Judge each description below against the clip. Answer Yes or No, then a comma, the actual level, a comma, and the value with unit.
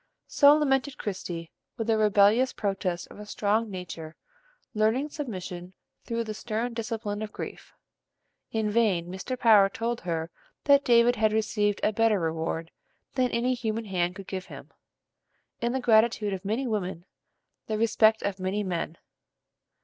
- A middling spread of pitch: Yes, average, 3.7 semitones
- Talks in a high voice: Yes, high, 215 Hz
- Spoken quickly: No, average, 150 wpm